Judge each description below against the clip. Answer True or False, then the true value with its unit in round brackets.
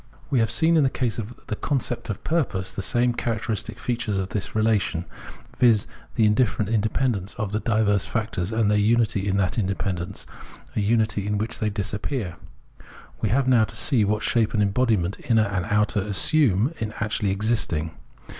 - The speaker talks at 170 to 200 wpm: True (175 wpm)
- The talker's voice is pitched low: True (110 Hz)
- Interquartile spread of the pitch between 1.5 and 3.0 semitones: True (2.6 semitones)